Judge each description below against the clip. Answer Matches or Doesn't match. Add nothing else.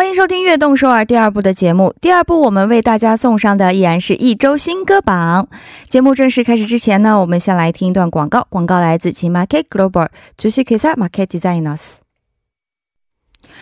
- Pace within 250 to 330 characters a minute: Doesn't match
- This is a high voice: Matches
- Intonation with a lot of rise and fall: Matches